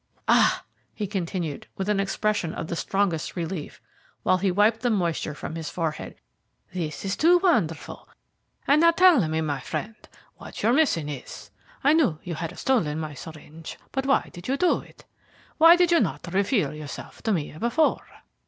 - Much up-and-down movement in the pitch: Yes, wide, 8.2 semitones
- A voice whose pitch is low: No, high, 190 Hz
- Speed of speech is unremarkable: Yes, average, 175 wpm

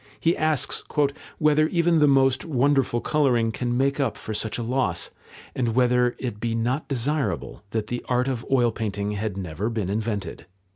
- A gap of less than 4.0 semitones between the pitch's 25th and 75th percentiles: Yes, average, 3.6 semitones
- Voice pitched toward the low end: Yes, low, 120 Hz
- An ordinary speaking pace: Yes, average, 175 wpm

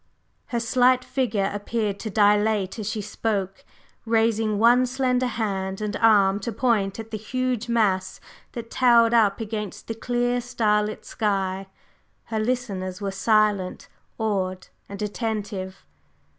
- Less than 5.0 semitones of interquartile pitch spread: Yes, average, 2.8 semitones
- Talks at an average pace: No, slow, 130 wpm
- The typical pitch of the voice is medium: No, high, 215 Hz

